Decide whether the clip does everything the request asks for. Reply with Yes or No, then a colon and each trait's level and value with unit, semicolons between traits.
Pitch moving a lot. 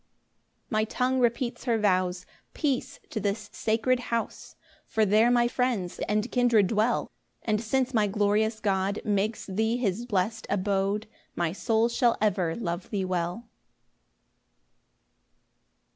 No: average, 3.2 semitones